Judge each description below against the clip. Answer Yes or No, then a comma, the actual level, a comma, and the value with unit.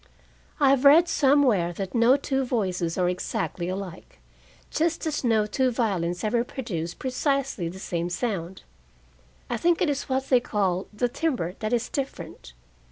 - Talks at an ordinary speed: Yes, average, 160 wpm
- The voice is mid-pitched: No, high, 230 Hz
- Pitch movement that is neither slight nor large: No, wide, 6.8 semitones